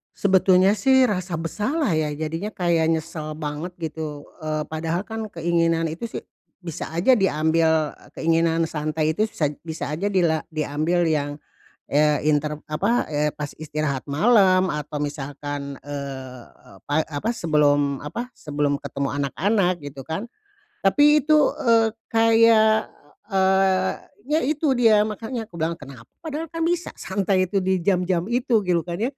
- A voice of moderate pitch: Yes, medium, 165 Hz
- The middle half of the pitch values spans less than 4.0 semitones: No, wide, 5.4 semitones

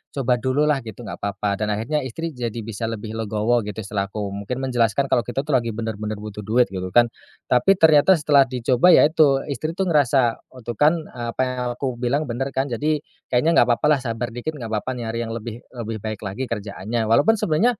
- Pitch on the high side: No, low, 120 Hz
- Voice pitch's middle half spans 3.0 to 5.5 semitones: Yes, average, 4.0 semitones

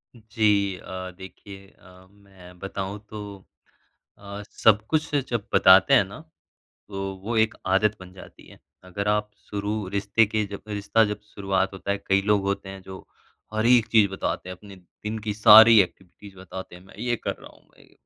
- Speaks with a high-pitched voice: No, low, 100 Hz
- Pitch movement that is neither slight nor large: No, narrow, 1.9 semitones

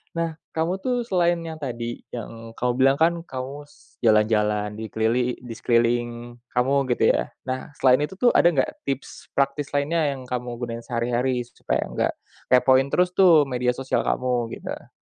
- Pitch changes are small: No, average, 3.7 semitones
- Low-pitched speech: Yes, low, 130 Hz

